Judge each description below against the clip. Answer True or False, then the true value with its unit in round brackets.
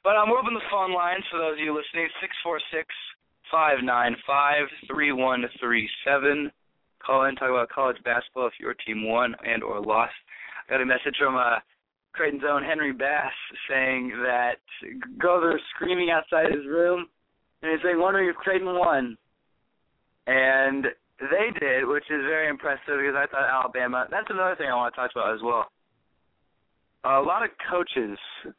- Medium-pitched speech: True (145 Hz)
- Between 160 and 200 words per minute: True (185 wpm)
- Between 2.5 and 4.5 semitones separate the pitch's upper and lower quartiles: False (5.2 semitones)